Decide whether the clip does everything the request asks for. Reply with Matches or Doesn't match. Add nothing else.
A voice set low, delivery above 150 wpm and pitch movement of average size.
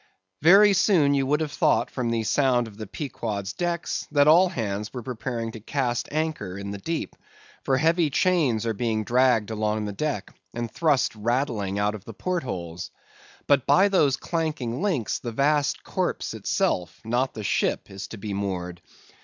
Doesn't match